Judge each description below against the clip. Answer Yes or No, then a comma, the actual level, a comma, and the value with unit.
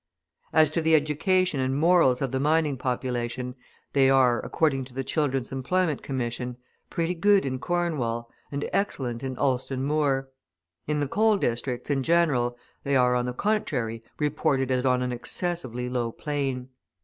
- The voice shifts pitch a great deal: No, average, 3.7 semitones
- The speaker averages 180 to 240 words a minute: No, average, 160 wpm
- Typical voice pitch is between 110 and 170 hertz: Yes, low, 135 Hz